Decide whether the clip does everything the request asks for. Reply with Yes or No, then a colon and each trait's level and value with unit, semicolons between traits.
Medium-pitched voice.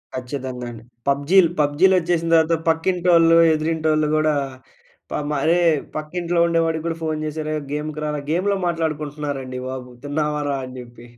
Yes: medium, 155 Hz